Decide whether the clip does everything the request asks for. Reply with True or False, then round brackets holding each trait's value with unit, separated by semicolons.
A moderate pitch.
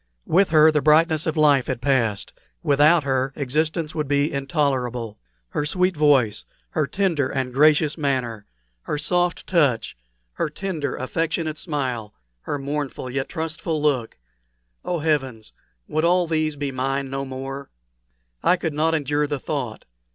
True (145 Hz)